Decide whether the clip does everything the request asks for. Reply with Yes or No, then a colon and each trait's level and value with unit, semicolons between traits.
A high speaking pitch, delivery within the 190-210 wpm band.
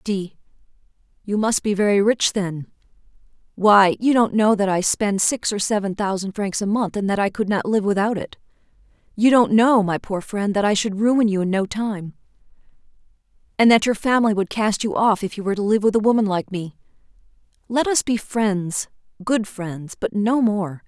Yes: high, 205 Hz; average, 200 wpm